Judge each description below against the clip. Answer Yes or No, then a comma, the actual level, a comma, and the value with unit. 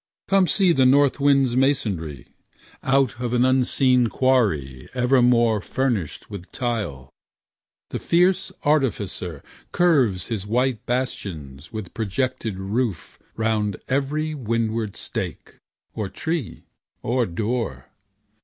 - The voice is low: Yes, low, 120 Hz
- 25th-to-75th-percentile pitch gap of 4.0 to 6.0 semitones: Yes, average, 4.7 semitones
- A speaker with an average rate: No, slow, 105 wpm